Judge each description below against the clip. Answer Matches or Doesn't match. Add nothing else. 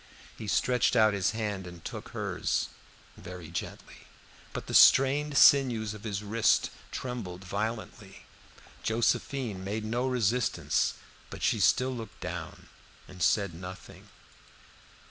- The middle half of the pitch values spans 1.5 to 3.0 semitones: Doesn't match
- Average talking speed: Doesn't match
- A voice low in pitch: Matches